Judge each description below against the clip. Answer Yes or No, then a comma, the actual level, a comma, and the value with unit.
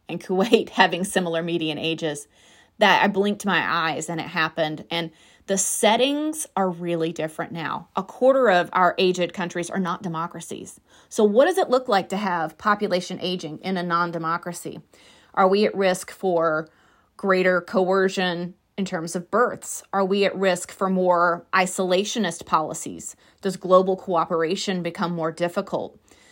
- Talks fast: No, average, 155 wpm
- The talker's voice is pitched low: No, medium, 185 Hz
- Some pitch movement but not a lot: No, narrow, 2.3 semitones